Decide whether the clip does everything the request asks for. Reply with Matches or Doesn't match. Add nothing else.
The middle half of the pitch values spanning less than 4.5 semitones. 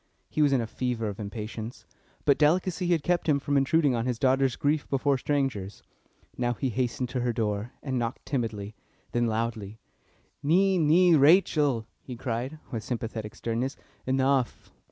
Matches